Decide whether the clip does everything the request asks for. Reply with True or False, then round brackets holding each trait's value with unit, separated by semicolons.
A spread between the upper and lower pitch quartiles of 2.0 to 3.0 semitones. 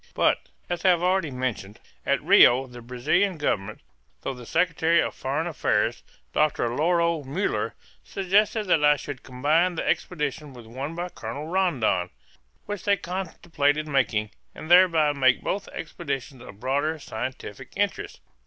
False (5.2 semitones)